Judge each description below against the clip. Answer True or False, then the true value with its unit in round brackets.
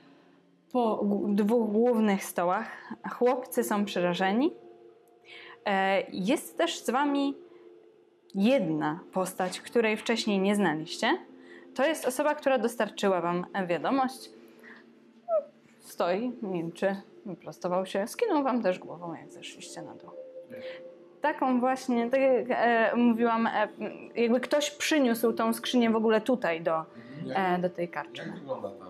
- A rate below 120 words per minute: True (110 wpm)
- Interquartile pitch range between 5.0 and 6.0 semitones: True (5.6 semitones)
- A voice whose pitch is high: True (230 Hz)